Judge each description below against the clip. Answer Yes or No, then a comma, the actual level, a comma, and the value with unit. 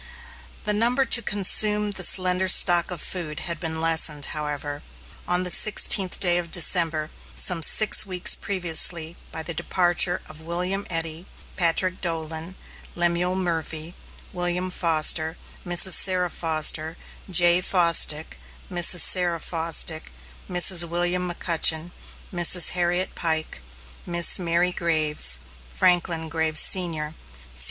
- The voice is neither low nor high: Yes, medium, 175 Hz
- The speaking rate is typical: No, slow, 115 wpm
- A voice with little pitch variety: Yes, narrow, 2.0 semitones